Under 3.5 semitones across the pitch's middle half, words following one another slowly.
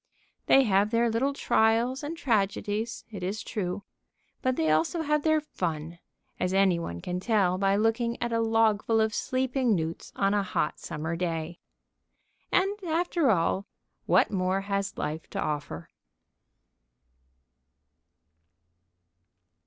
No: average, 4.9 semitones; slow, 130 wpm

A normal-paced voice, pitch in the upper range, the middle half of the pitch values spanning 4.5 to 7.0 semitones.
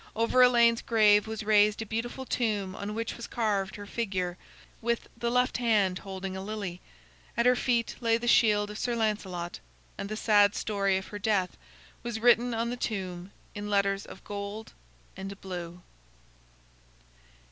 No: average, 165 wpm; high, 210 Hz; average, 2.9 semitones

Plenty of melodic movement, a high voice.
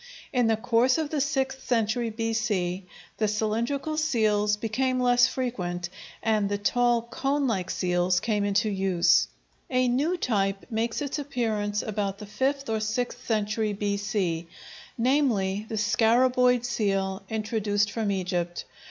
No: average, 3.5 semitones; high, 220 Hz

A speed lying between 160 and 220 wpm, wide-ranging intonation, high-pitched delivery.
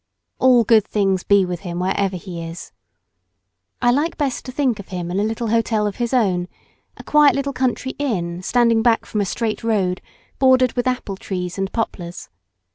No: average, 190 wpm; average, 5.0 semitones; high, 215 Hz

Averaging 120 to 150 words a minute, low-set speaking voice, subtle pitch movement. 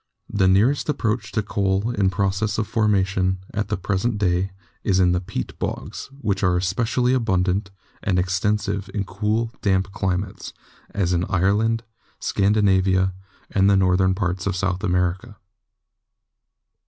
Yes: average, 140 wpm; very low, 95 Hz; narrow, 2.1 semitones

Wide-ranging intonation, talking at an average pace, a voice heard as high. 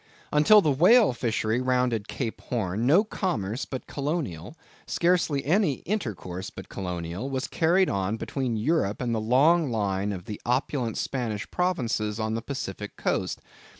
No: wide, 6.4 semitones; average, 150 wpm; low, 125 Hz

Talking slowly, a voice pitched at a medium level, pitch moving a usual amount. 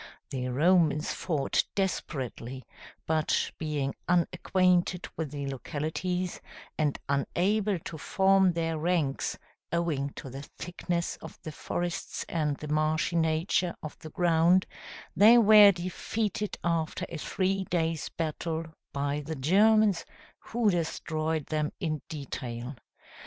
Yes: slow, 120 wpm; medium, 165 Hz; average, 3.3 semitones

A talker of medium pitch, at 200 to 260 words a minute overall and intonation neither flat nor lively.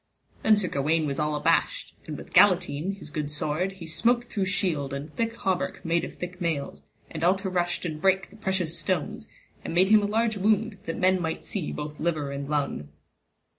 Yes: medium, 175 Hz; fast, 205 wpm; average, 4.2 semitones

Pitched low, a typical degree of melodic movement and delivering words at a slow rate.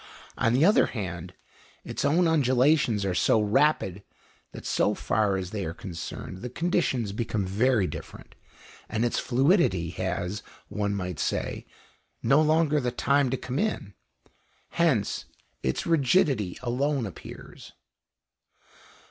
No: low, 120 Hz; wide, 6.7 semitones; slow, 130 wpm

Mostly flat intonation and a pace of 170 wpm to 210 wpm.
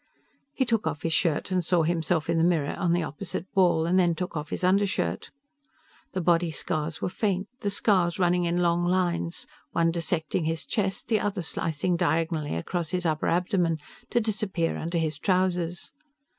Yes: narrow, 2.2 semitones; average, 185 wpm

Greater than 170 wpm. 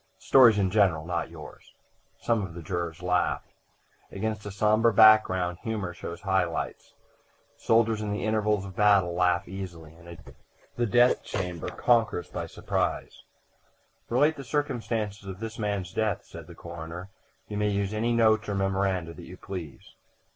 No: average, 165 wpm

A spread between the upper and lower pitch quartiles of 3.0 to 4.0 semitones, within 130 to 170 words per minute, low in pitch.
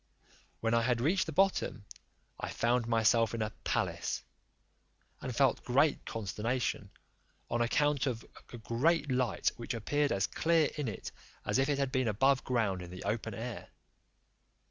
Yes: average, 3.6 semitones; average, 160 wpm; low, 120 Hz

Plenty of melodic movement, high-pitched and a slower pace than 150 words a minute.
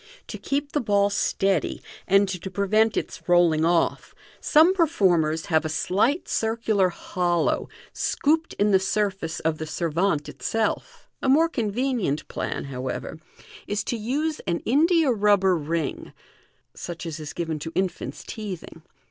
Yes: wide, 5.8 semitones; high, 195 Hz; average, 140 wpm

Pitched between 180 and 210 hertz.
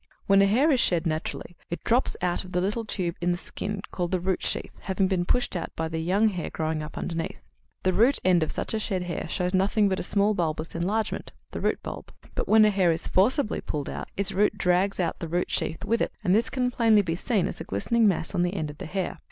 Yes: medium, 185 Hz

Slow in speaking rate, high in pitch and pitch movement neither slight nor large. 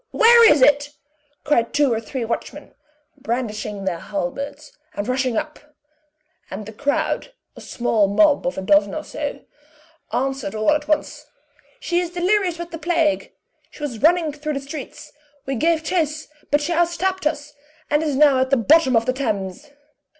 No: average, 170 wpm; very high, 290 Hz; average, 4.5 semitones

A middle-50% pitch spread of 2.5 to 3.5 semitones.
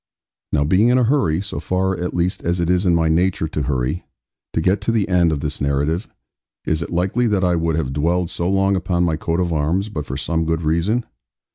Yes: average, 2.9 semitones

